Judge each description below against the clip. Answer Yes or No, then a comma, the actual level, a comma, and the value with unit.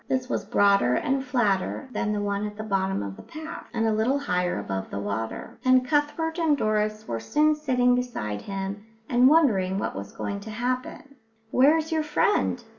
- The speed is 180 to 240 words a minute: Yes, average, 190 wpm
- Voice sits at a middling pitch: No, high, 225 Hz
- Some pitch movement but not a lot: No, wide, 6.1 semitones